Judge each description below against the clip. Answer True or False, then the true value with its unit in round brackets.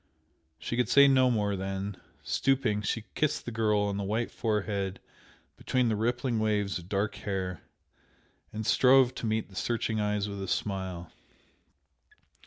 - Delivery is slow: False (155 wpm)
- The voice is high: False (105 Hz)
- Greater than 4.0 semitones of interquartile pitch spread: False (3.0 semitones)